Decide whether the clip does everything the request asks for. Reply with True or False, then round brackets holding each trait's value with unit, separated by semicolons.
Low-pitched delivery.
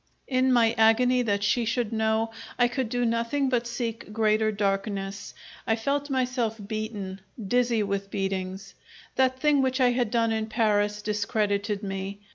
False (225 Hz)